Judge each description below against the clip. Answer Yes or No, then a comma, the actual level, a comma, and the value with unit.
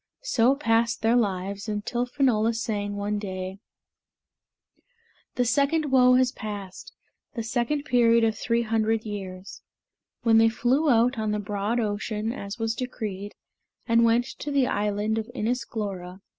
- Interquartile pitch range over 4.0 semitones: No, average, 2.9 semitones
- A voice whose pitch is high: Yes, high, 225 Hz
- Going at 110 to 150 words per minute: Yes, average, 145 wpm